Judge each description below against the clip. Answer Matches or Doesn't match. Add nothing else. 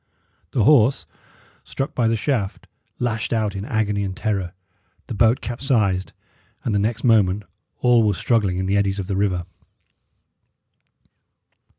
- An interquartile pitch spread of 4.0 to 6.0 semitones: Doesn't match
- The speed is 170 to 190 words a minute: Doesn't match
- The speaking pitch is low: Matches